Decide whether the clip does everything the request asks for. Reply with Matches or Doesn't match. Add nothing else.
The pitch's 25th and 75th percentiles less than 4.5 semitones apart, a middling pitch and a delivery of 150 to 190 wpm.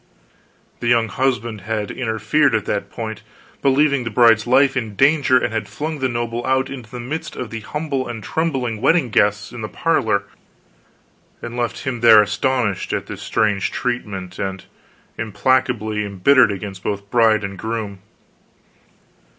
Doesn't match